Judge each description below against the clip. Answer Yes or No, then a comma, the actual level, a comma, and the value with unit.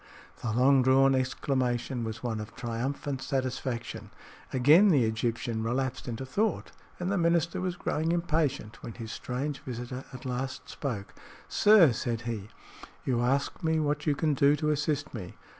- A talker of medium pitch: No, low, 130 Hz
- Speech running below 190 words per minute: Yes, average, 160 wpm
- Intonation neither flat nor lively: Yes, average, 3.9 semitones